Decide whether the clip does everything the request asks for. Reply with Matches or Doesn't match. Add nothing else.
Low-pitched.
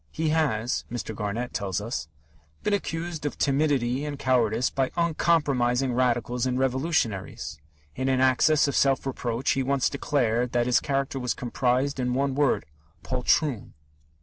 Matches